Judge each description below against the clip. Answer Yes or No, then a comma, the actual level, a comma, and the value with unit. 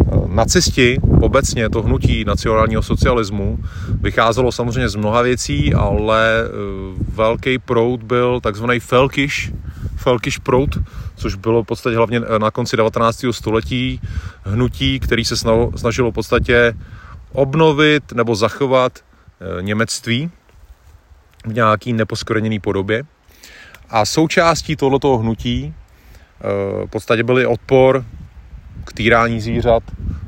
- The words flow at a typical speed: No, slow, 105 wpm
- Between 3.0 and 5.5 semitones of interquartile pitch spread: Yes, average, 3.4 semitones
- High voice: No, low, 115 Hz